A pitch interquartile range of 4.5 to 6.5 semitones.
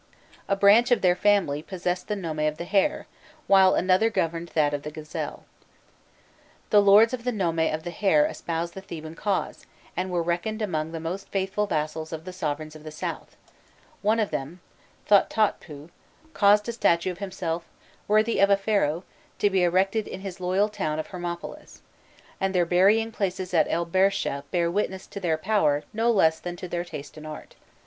No: average, 3.8 semitones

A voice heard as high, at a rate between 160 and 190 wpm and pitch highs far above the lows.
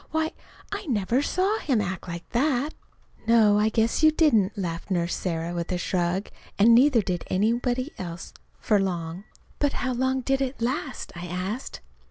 Yes: high, 220 Hz; average, 170 wpm; wide, 6.4 semitones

